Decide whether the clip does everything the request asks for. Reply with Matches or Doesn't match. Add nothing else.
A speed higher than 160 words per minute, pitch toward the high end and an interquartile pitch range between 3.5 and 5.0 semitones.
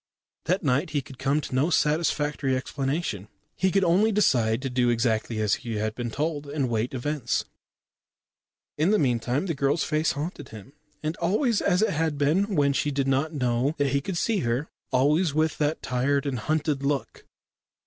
Doesn't match